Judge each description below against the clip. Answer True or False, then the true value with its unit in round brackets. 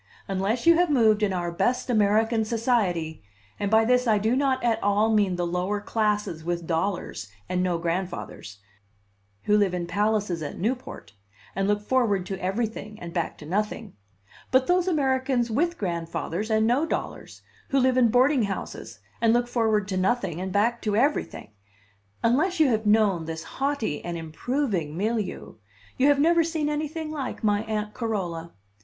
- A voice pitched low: False (215 Hz)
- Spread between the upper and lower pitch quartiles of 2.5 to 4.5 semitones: False (5.3 semitones)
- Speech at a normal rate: True (170 wpm)